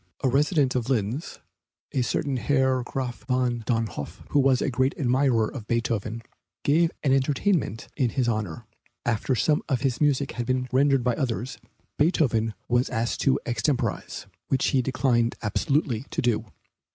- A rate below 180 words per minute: Yes, average, 155 wpm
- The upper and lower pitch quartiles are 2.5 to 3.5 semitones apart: Yes, average, 2.8 semitones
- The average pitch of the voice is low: Yes, low, 125 Hz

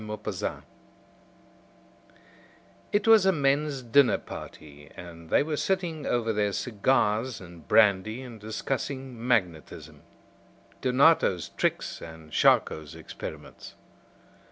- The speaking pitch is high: No, low, 115 Hz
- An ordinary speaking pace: No, slow, 100 wpm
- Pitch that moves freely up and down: Yes, wide, 7.3 semitones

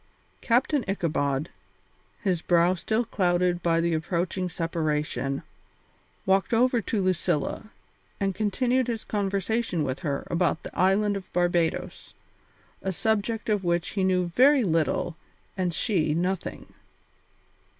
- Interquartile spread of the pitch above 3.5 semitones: Yes, average, 3.9 semitones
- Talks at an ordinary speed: No, slow, 120 wpm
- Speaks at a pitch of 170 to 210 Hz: Yes, medium, 185 Hz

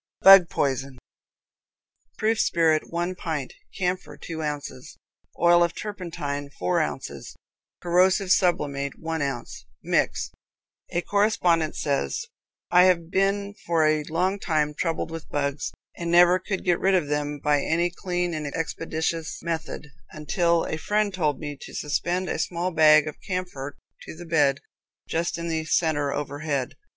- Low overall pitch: No, medium, 165 Hz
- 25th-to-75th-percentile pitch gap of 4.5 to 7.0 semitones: No, average, 3.3 semitones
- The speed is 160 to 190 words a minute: No, average, 145 wpm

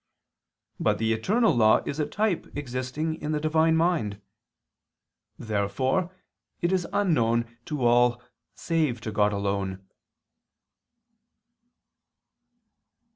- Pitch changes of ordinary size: No, wide, 6.6 semitones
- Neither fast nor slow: No, slow, 95 wpm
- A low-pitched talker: Yes, low, 130 Hz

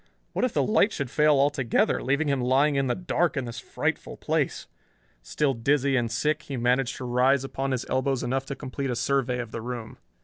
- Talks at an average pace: No, fast, 210 wpm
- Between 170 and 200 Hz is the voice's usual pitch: No, low, 135 Hz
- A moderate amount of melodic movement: No, narrow, 2.3 semitones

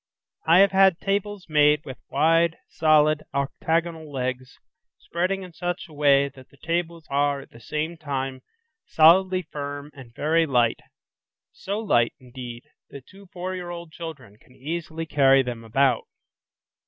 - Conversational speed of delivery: Yes, average, 150 wpm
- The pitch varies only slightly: No, average, 4.1 semitones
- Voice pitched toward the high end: No, medium, 155 Hz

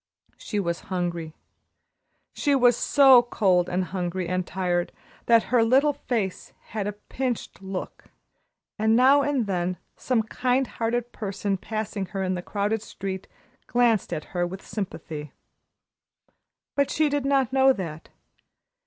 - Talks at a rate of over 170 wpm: No, average, 145 wpm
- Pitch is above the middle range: Yes, high, 205 Hz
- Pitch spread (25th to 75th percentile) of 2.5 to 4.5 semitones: No, average, 5.2 semitones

